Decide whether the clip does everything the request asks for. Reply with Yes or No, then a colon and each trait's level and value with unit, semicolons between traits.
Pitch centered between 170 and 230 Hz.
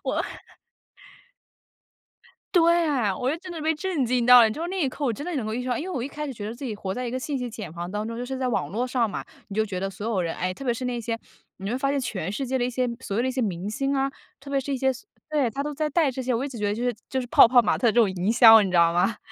No: high, 245 Hz